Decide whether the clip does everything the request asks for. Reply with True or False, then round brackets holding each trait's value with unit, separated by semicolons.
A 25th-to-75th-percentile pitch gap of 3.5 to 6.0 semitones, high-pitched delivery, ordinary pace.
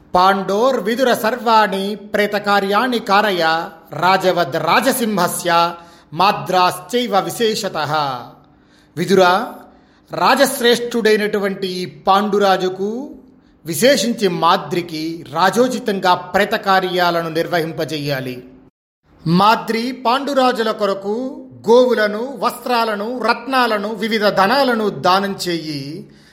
False (4.7 semitones; 200 Hz; 55 wpm)